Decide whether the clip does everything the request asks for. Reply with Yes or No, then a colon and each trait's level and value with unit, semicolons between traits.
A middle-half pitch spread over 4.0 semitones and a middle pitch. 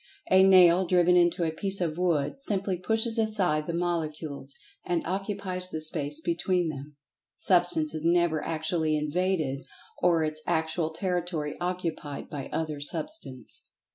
No: average, 2.9 semitones; medium, 170 Hz